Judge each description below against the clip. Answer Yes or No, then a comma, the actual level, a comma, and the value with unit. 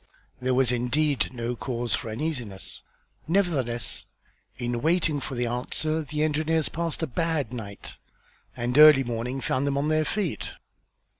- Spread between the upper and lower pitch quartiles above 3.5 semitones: Yes, average, 4.4 semitones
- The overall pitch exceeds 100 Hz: Yes, low, 135 Hz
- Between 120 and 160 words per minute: Yes, average, 145 wpm